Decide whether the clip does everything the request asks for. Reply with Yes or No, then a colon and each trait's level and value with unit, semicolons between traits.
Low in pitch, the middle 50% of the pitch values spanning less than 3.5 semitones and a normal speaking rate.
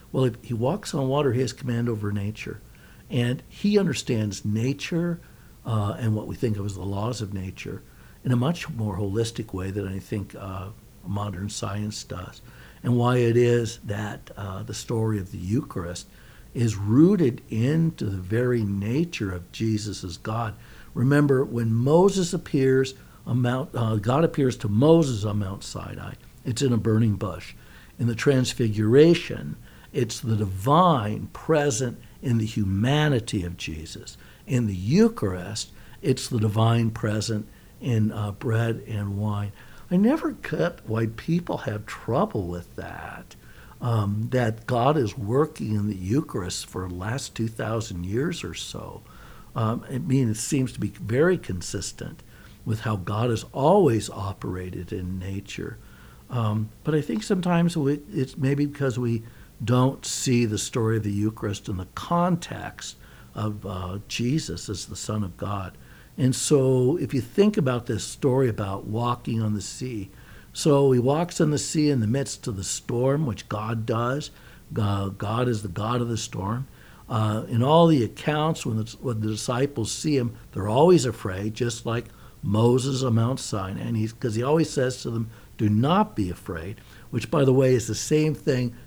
No: low, 115 Hz; average, 4.1 semitones; average, 170 wpm